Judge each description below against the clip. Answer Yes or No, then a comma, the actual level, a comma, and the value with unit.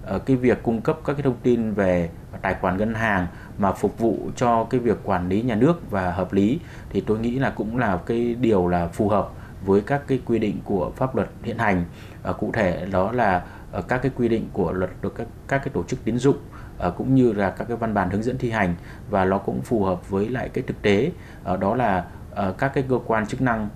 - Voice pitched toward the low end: Yes, low, 110 Hz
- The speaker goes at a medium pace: Yes, average, 240 wpm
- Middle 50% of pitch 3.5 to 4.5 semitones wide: Yes, average, 4.2 semitones